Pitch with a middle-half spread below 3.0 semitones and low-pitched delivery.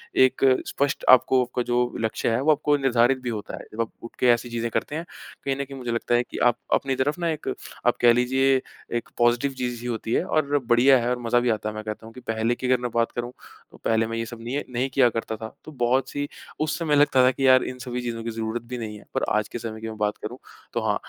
Yes: narrow, 2.5 semitones; low, 120 Hz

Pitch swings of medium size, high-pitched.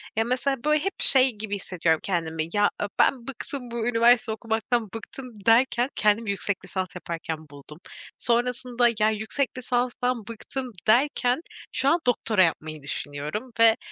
Yes: average, 4.0 semitones; high, 230 Hz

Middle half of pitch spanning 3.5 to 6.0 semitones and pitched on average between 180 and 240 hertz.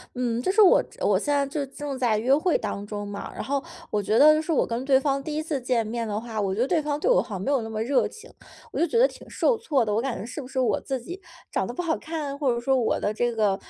No: average, 4.9 semitones; very high, 265 Hz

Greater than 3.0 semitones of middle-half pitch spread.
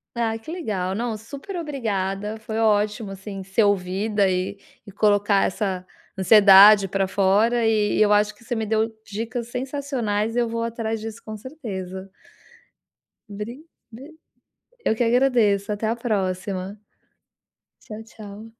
No: narrow, 2.6 semitones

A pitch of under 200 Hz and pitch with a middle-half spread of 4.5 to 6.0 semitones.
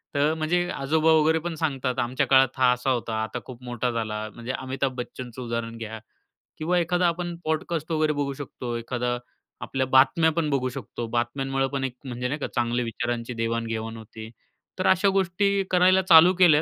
Yes: low, 135 Hz; average, 4.9 semitones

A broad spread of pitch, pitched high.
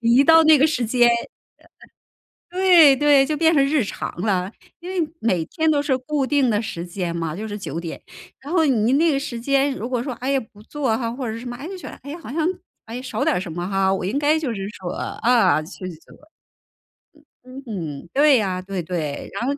Yes: wide, 7.0 semitones; high, 245 Hz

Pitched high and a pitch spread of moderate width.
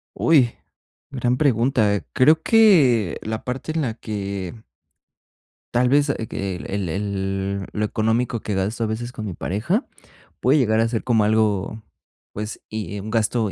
No: low, 110 Hz; average, 3.6 semitones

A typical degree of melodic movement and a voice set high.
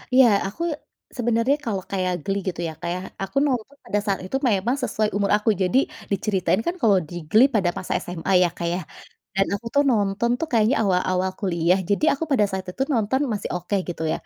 Yes: average, 4.1 semitones; high, 200 Hz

